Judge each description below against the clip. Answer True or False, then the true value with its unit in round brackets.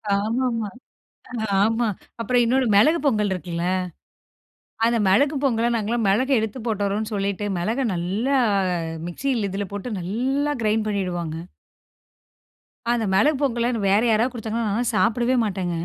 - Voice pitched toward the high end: True (220 Hz)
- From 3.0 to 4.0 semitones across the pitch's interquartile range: True (3.3 semitones)